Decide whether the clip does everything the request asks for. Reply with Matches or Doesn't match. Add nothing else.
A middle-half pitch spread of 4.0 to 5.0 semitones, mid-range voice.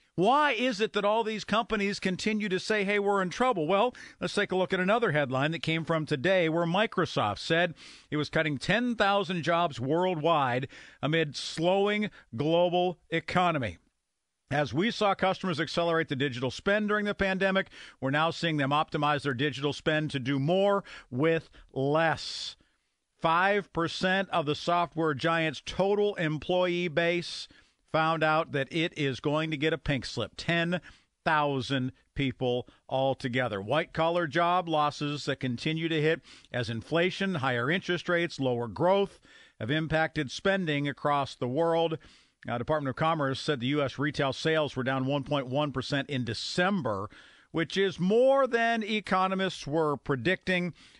Matches